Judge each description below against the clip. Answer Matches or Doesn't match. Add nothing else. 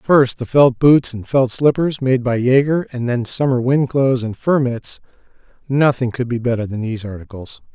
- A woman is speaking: Doesn't match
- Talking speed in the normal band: Matches